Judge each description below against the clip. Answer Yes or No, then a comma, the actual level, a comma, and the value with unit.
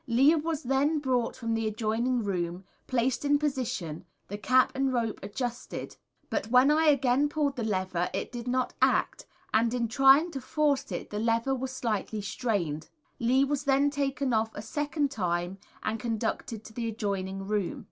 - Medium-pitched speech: No, high, 245 Hz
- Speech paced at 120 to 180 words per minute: Yes, average, 175 wpm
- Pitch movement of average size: Yes, average, 4.0 semitones